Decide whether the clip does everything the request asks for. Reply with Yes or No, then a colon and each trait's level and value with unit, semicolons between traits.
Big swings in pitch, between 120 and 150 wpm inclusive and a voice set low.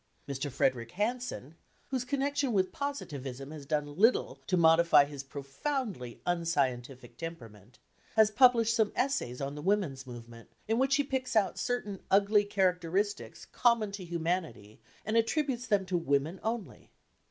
No: wide, 8.5 semitones; average, 140 wpm; medium, 185 Hz